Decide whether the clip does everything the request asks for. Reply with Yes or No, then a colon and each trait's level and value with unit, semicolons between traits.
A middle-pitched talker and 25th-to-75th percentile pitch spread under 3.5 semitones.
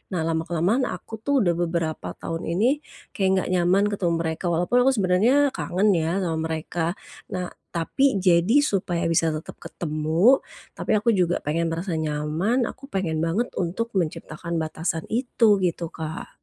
Yes: medium, 170 Hz; average, 3.0 semitones